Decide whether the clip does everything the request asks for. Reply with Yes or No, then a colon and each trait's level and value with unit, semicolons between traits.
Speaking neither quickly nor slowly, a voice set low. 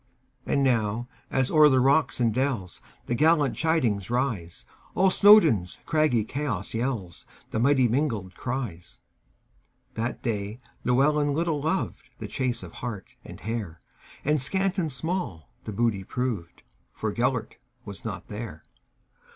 No: slow, 115 wpm; low, 125 Hz